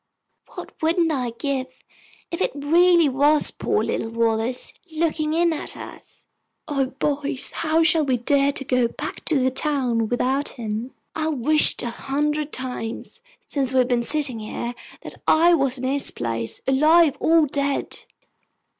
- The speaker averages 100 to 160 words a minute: Yes, average, 155 wpm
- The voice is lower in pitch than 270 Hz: No, very high, 275 Hz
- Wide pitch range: No, average, 3.6 semitones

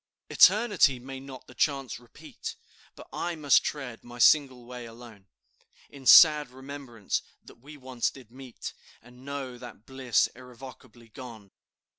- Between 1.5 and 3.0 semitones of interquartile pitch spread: Yes, narrow, 2.4 semitones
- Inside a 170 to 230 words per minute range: No, average, 140 wpm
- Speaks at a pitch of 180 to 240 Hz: No, low, 130 Hz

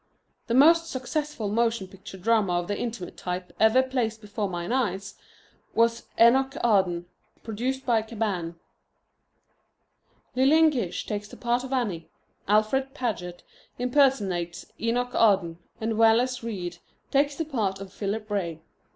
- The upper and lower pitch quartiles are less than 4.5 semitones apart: No, average, 4.8 semitones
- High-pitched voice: Yes, high, 225 Hz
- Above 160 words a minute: No, slow, 135 wpm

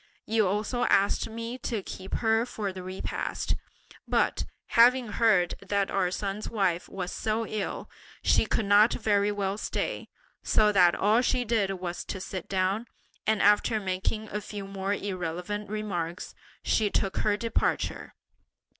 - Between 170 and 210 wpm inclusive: No, average, 150 wpm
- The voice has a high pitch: Yes, high, 205 Hz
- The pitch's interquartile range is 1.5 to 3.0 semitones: Yes, narrow, 2.4 semitones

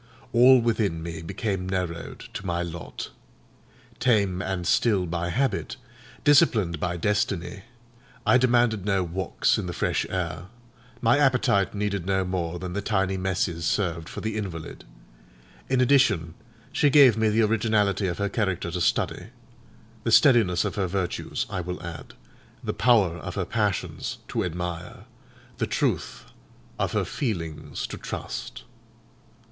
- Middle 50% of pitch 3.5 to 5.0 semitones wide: Yes, average, 4.1 semitones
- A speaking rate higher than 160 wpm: No, average, 145 wpm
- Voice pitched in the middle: No, very low, 95 Hz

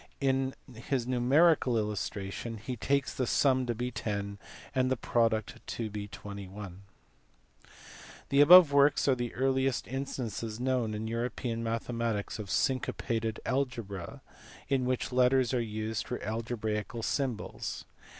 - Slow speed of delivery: Yes, slow, 120 wpm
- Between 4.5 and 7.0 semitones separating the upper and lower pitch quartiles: No, average, 3.3 semitones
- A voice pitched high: No, low, 120 Hz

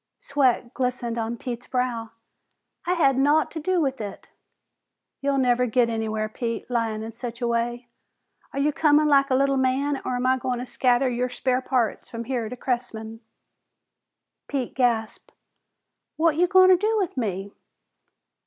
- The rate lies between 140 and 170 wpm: Yes, average, 165 wpm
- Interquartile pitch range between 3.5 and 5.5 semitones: No, average, 2.9 semitones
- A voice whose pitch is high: Yes, very high, 250 Hz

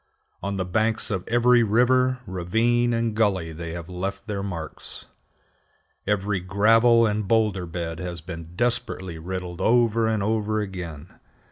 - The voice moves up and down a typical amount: Yes, average, 4.1 semitones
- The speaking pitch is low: Yes, low, 100 Hz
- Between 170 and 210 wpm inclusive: No, average, 140 wpm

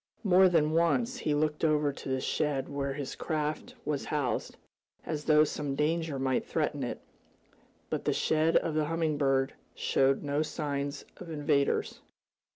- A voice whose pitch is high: No, medium, 150 Hz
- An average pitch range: No, narrow, 2.1 semitones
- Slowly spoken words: No, average, 160 wpm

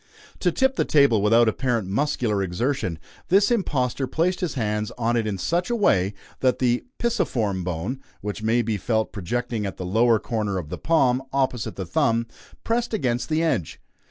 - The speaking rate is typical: Yes, average, 180 wpm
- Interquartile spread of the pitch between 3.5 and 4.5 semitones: No, average, 5.0 semitones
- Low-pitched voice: Yes, low, 120 Hz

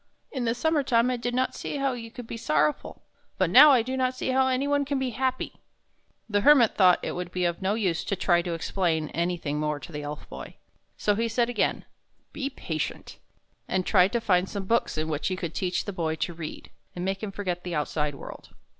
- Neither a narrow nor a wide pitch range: No, wide, 6.4 semitones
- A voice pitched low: No, high, 195 Hz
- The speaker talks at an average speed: No, fast, 235 wpm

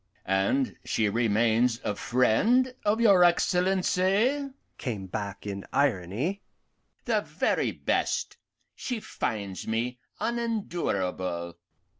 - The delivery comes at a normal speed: No, slow, 95 wpm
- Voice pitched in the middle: No, low, 125 Hz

